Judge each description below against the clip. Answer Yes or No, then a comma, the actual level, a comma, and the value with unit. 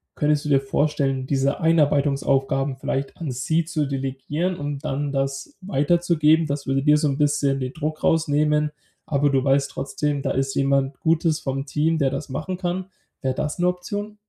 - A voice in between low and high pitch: Yes, medium, 145 Hz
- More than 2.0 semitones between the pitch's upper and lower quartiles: Yes, narrow, 2.5 semitones